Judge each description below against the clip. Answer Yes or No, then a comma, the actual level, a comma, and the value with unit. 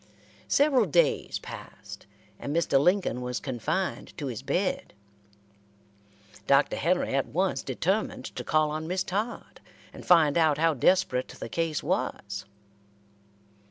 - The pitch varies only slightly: No, average, 5.1 semitones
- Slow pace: Yes, slow, 125 wpm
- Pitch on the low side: No, medium, 160 Hz